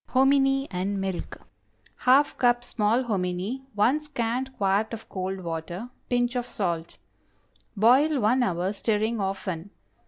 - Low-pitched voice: No, high, 220 Hz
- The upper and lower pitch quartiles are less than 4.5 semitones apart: No, average, 4.8 semitones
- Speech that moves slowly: Yes, slow, 130 wpm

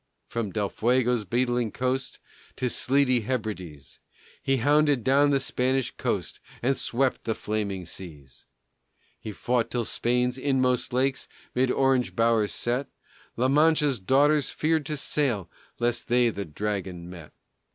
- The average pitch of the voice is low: Yes, low, 125 Hz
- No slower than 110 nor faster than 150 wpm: Yes, average, 140 wpm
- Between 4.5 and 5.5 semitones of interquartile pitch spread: No, average, 3.8 semitones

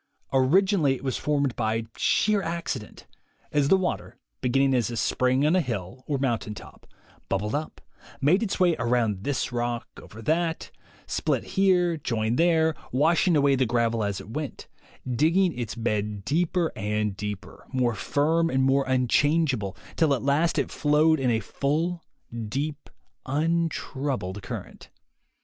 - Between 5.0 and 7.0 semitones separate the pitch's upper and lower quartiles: Yes, wide, 5.6 semitones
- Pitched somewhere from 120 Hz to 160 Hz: Yes, low, 135 Hz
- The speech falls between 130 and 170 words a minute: Yes, average, 150 wpm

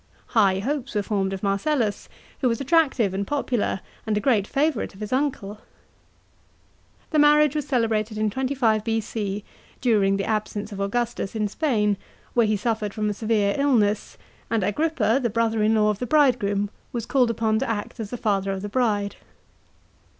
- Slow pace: No, average, 175 wpm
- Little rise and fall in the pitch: No, average, 3.4 semitones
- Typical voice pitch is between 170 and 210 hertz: No, high, 220 Hz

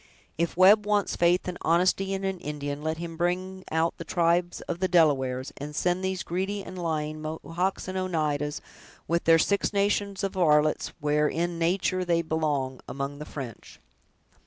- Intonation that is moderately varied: Yes, average, 3.6 semitones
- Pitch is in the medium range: Yes, medium, 170 Hz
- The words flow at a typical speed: Yes, average, 170 wpm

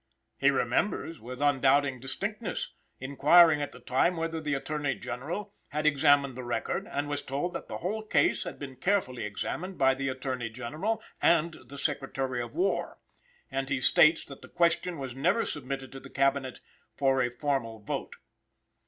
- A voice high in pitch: No, medium, 140 Hz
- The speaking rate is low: No, average, 170 wpm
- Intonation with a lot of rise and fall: No, average, 3.7 semitones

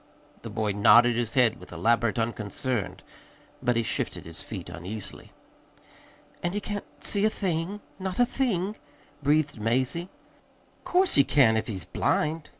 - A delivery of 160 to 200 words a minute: No, average, 150 wpm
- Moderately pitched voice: No, low, 125 Hz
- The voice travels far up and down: Yes, wide, 8.1 semitones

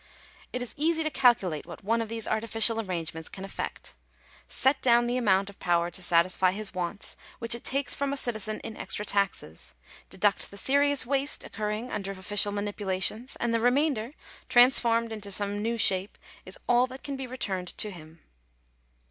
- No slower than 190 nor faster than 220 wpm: No, average, 175 wpm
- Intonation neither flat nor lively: Yes, average, 4.4 semitones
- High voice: Yes, high, 215 Hz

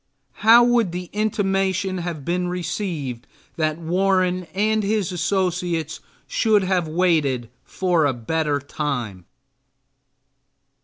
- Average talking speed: No, slow, 100 wpm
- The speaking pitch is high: No, medium, 180 Hz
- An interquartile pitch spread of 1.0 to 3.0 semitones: No, average, 3.7 semitones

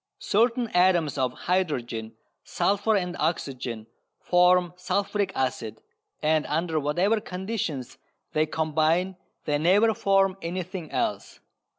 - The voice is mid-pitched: Yes, medium, 175 Hz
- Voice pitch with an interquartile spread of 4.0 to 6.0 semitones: Yes, average, 4.4 semitones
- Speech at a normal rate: No, slow, 105 wpm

